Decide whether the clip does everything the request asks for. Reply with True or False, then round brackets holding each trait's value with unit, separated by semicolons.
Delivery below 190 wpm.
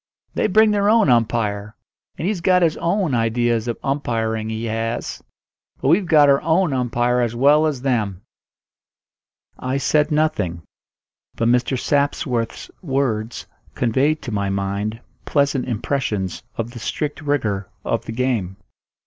True (140 wpm)